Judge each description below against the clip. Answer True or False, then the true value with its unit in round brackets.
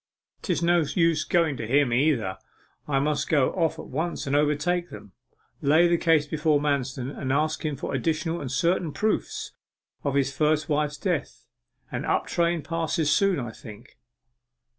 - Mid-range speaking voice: True (150 Hz)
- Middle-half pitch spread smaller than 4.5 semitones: True (3.2 semitones)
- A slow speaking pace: False (165 wpm)